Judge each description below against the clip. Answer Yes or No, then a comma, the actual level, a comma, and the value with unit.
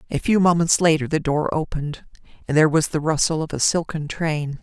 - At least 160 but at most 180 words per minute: No, fast, 205 wpm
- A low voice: No, medium, 155 Hz